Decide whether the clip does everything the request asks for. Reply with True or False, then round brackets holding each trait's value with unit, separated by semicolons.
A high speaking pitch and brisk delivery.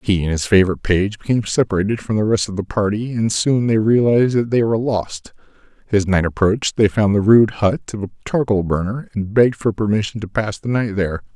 False (105 Hz; 220 wpm)